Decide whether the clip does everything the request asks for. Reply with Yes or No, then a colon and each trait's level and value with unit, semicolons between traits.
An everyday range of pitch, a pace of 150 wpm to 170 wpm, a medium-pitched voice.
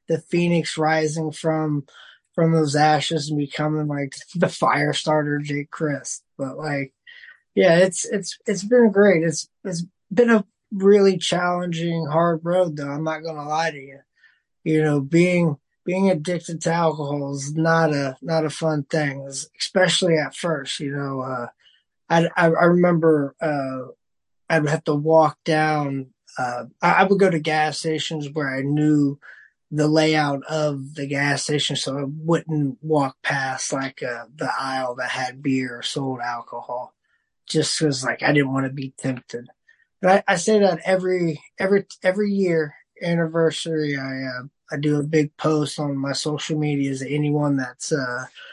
Yes: average, 3.1 semitones; average, 165 wpm; medium, 155 Hz